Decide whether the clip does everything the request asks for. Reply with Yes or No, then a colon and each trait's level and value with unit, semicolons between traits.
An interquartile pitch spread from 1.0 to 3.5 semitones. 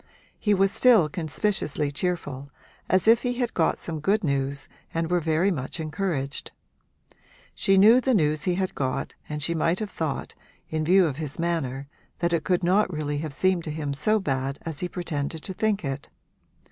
No: average, 4.5 semitones